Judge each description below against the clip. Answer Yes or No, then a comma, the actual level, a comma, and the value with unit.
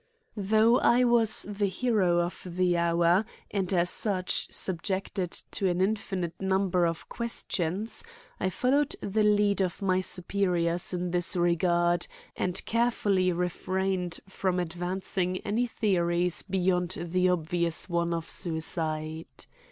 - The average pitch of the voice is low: No, medium, 180 Hz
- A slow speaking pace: Yes, slow, 125 wpm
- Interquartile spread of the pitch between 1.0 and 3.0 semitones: Yes, narrow, 2.4 semitones